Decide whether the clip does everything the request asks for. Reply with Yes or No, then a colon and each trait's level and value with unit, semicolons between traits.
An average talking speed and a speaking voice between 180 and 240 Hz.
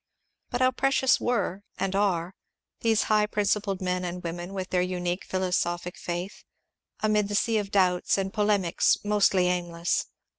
Yes: average, 150 wpm; high, 190 Hz